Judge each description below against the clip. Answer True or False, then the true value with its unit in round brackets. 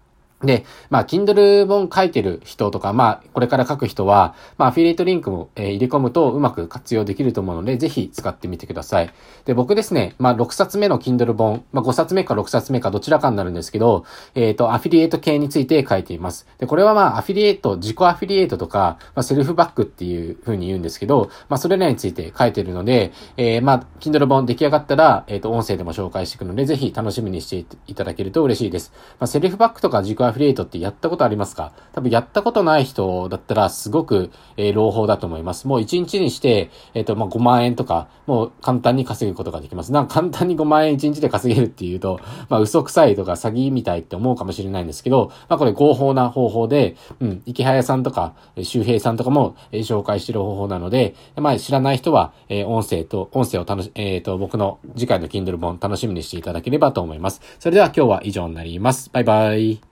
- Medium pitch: False (120 Hz)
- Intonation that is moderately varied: False (6.0 semitones)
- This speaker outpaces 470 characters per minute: True (480 characters per minute)